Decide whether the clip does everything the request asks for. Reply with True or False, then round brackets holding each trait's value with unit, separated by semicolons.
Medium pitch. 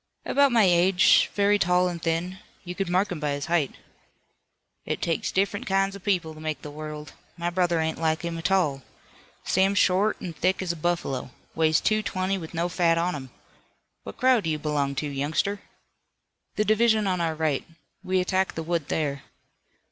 True (175 Hz)